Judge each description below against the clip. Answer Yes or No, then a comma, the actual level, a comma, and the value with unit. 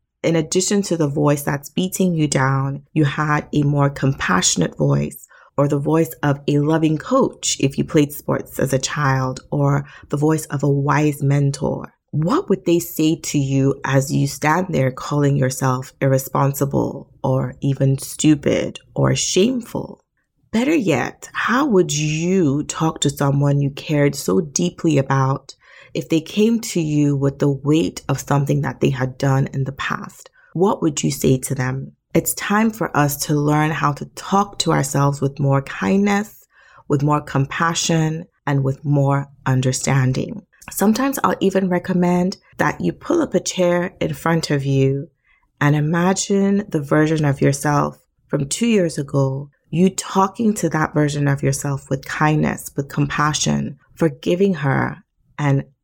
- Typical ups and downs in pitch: Yes, average, 3.4 semitones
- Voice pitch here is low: No, medium, 145 Hz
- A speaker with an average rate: Yes, average, 160 wpm